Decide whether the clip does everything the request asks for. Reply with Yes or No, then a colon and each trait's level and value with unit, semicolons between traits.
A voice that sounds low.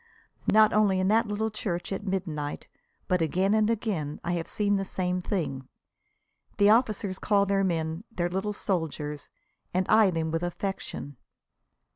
No: high, 190 Hz